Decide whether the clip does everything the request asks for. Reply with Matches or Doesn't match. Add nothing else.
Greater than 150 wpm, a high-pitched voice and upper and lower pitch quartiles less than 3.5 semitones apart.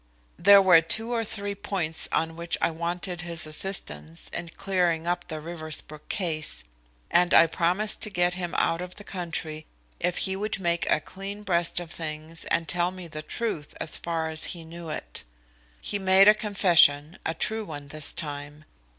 Doesn't match